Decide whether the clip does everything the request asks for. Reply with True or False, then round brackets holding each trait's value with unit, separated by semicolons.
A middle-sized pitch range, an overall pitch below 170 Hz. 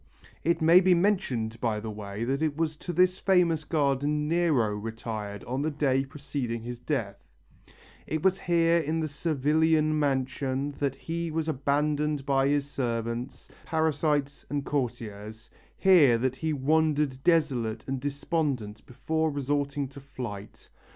True (4.3 semitones; 140 Hz)